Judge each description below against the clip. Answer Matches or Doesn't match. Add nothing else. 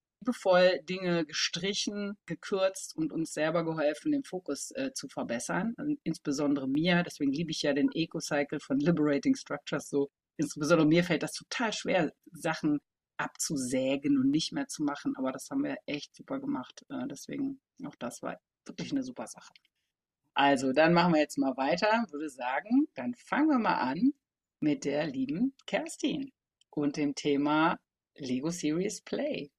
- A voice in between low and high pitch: Matches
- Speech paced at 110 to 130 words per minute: Doesn't match